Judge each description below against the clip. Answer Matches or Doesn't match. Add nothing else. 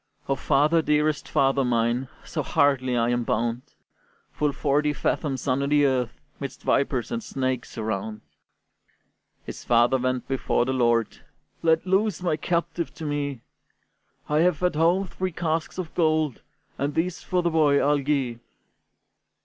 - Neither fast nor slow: Matches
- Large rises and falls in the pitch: Doesn't match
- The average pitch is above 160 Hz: Doesn't match